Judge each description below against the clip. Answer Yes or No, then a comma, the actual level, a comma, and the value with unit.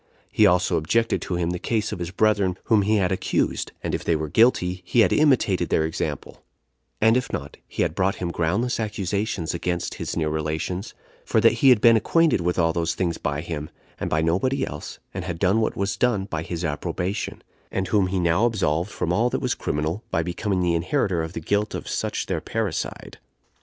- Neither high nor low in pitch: No, very low, 90 Hz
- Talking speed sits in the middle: No, fast, 210 wpm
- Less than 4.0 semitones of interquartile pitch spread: No, average, 4.5 semitones